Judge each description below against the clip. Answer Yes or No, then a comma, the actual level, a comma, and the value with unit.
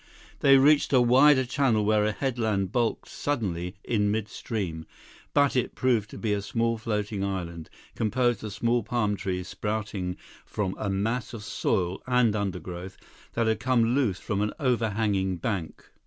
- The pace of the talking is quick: No, average, 155 wpm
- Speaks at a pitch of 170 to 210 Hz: No, low, 110 Hz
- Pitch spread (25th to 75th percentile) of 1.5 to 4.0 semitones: Yes, average, 3.7 semitones